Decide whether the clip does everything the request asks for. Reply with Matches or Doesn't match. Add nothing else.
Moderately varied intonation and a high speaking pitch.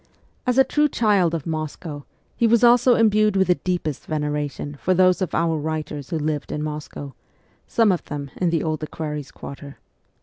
Doesn't match